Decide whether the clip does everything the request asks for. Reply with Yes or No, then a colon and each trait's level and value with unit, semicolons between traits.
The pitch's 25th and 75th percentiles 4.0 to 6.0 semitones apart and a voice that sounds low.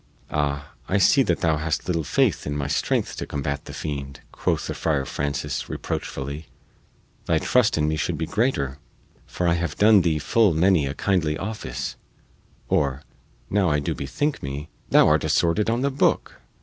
Yes: average, 4.8 semitones; very low, 80 Hz